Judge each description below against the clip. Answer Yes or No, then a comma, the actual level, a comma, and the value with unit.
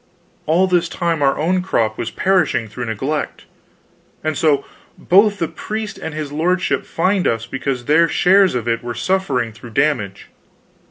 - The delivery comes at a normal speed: Yes, average, 160 wpm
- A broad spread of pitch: Yes, wide, 7.0 semitones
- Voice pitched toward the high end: No, medium, 155 Hz